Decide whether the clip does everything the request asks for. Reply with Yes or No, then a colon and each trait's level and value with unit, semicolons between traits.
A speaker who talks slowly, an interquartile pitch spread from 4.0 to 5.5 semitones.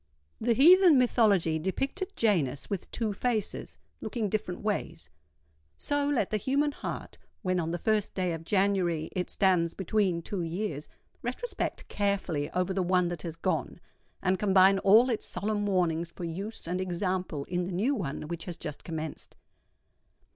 No: average, 155 wpm; average, 4.3 semitones